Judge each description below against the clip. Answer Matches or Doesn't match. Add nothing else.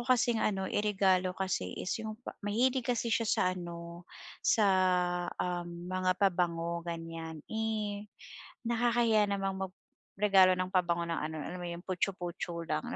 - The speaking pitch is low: Doesn't match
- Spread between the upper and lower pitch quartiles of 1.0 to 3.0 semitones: Doesn't match